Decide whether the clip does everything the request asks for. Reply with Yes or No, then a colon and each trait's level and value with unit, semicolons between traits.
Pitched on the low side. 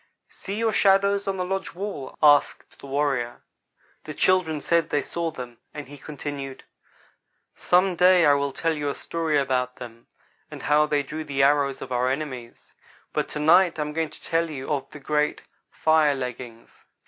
No: medium, 150 Hz